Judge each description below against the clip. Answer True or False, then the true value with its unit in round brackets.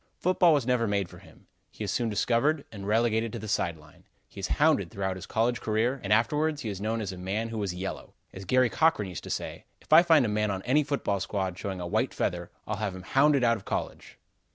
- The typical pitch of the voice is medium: False (110 Hz)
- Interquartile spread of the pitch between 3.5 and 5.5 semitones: True (4.7 semitones)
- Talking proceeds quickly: True (245 wpm)